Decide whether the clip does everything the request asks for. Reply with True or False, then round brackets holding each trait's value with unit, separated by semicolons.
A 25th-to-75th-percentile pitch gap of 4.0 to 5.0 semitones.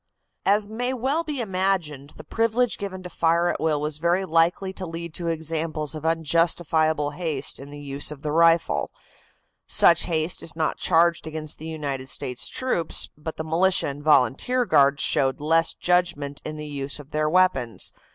False (3.2 semitones)